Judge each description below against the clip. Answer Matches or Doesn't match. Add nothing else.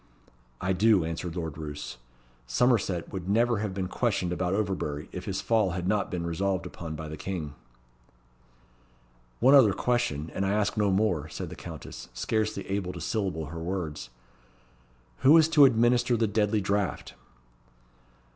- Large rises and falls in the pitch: Doesn't match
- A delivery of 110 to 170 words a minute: Matches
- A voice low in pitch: Matches